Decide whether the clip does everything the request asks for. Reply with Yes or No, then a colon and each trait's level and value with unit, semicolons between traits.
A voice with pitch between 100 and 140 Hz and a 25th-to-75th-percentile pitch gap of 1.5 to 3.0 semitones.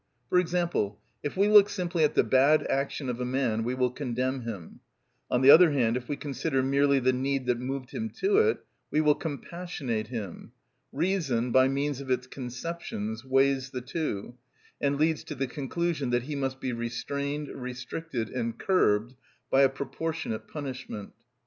No: low, 135 Hz; average, 3.4 semitones